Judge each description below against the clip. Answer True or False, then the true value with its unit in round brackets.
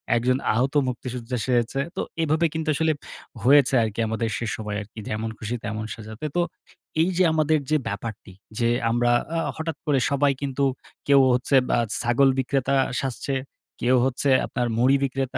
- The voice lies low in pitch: True (130 Hz)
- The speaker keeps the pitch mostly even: False (3.3 semitones)